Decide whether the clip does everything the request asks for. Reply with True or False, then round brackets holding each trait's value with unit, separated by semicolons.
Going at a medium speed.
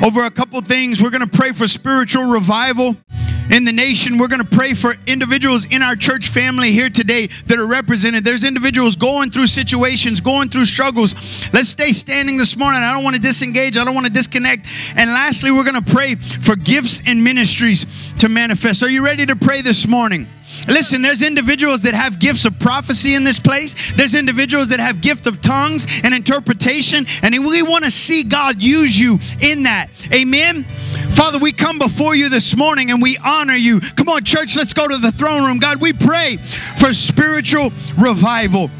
True (190 wpm)